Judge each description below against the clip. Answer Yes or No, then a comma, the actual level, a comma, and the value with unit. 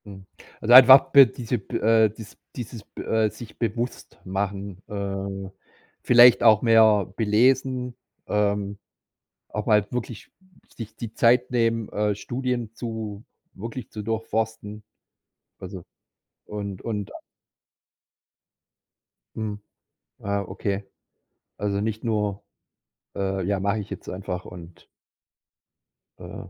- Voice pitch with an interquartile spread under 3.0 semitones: Yes, narrow, 2.4 semitones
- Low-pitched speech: Yes, low, 105 Hz